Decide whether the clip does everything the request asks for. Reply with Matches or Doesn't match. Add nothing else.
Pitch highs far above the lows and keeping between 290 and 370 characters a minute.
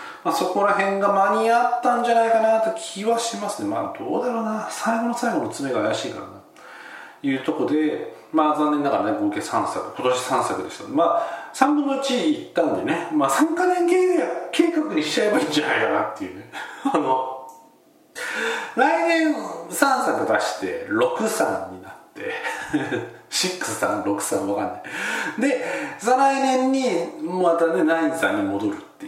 Matches